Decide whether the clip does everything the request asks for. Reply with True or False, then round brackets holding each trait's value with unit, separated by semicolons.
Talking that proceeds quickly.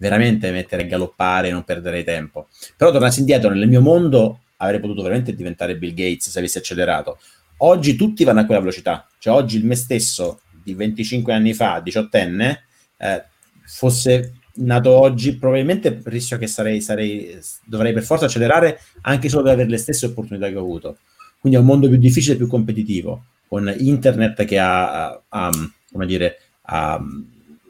True (175 wpm)